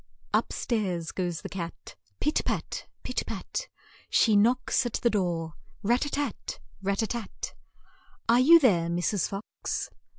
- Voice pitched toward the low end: No, high, 210 Hz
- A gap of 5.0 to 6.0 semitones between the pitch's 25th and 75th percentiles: Yes, wide, 5.6 semitones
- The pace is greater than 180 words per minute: No, average, 145 wpm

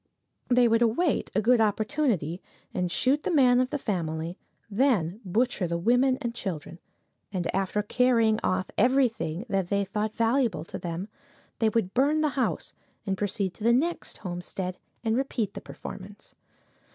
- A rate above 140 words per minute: Yes, average, 160 wpm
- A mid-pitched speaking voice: No, high, 215 Hz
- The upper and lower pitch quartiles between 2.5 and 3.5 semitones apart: No, average, 5.0 semitones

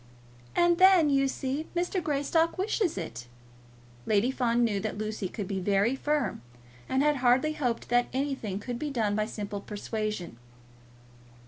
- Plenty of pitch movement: Yes, wide, 6.1 semitones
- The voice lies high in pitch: Yes, high, 245 Hz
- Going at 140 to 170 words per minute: Yes, average, 150 wpm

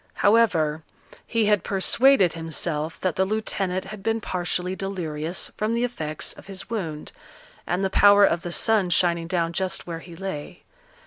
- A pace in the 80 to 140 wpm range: No, average, 165 wpm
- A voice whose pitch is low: No, medium, 185 Hz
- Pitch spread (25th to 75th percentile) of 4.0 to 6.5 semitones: No, average, 3.5 semitones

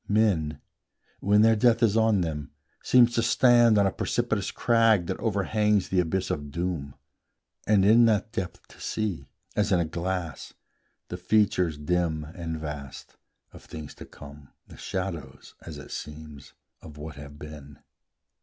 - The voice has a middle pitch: No, very low, 90 Hz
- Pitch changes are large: Yes, wide, 5.9 semitones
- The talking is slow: No, average, 155 wpm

